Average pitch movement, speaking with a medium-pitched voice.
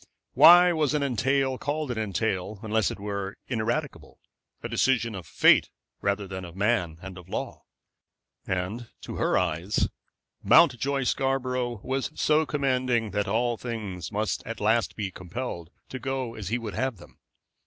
No: average, 4.9 semitones; low, 115 Hz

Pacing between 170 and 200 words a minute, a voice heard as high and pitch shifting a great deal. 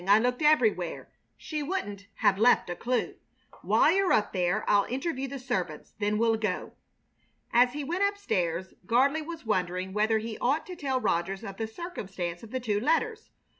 Yes: average, 180 wpm; high, 225 Hz; wide, 6.7 semitones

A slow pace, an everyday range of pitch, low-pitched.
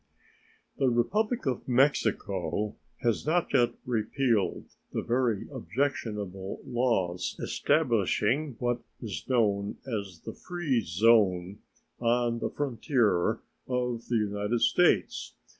Yes: slow, 105 wpm; average, 4.0 semitones; low, 115 Hz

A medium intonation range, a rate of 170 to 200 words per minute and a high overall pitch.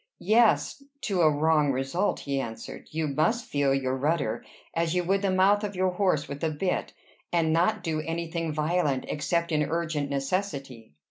No: average, 4.2 semitones; average, 180 wpm; medium, 160 Hz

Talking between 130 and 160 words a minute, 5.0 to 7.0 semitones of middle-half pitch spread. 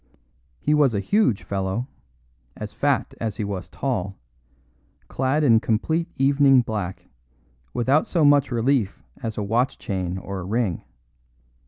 Yes: average, 140 wpm; wide, 5.6 semitones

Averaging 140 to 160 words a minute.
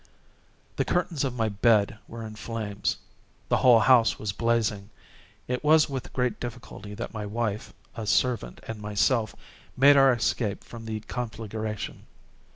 Yes: average, 150 wpm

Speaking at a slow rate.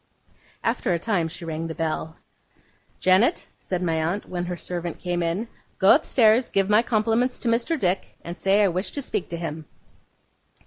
No: average, 180 wpm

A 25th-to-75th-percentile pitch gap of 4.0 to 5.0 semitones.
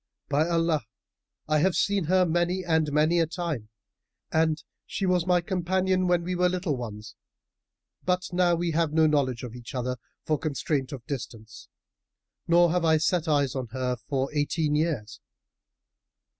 Yes: average, 4.3 semitones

